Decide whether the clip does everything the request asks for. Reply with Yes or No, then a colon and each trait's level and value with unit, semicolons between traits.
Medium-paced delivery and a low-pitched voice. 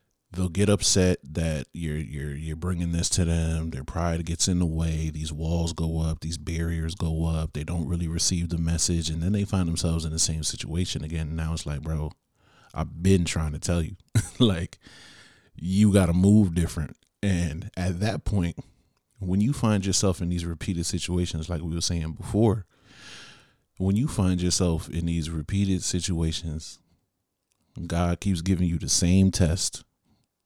Yes: average, 175 wpm; very low, 85 Hz